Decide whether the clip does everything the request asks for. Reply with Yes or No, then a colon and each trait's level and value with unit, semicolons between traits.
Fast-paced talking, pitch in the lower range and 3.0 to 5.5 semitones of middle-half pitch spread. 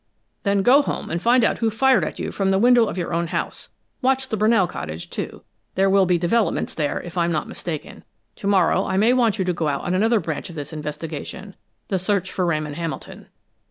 No: fast, 225 wpm; high, 190 Hz; average, 4.7 semitones